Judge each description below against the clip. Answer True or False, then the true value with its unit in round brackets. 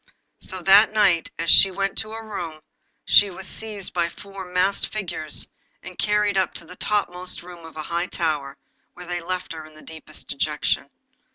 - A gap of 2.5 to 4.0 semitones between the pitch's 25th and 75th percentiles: True (2.9 semitones)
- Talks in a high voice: False (180 Hz)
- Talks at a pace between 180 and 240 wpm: True (185 wpm)